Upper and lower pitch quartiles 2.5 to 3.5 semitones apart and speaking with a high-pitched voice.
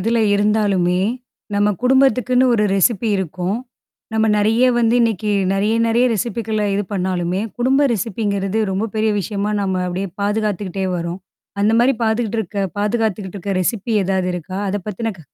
Yes: average, 2.9 semitones; high, 210 Hz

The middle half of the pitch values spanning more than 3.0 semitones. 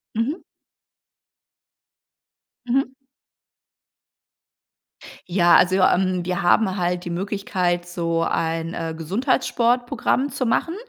Yes: average, 5.0 semitones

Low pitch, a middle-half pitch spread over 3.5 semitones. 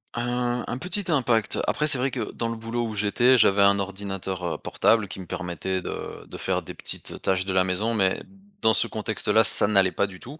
Yes: low, 105 Hz; average, 4.0 semitones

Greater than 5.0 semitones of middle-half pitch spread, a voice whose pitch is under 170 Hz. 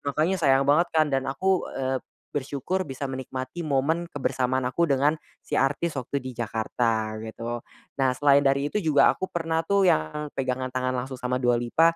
No: average, 3.2 semitones; low, 135 Hz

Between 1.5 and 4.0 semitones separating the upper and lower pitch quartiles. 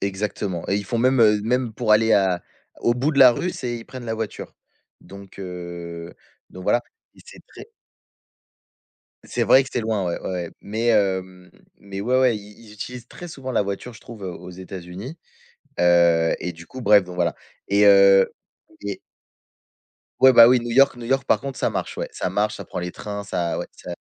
No: average, 4.5 semitones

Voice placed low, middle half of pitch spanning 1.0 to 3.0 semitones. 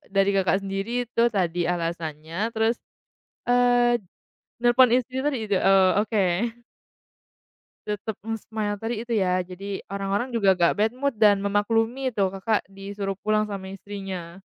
No: high, 205 Hz; average, 2.7 semitones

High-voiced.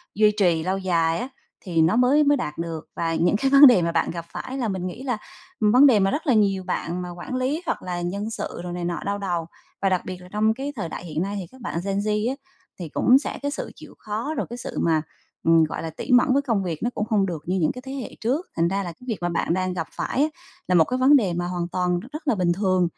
Yes: high, 195 Hz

